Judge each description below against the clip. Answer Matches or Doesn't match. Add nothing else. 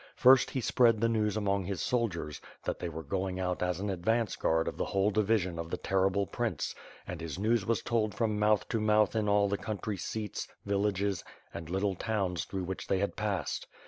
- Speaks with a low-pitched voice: Matches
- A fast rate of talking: Matches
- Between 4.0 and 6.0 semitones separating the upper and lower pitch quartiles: Doesn't match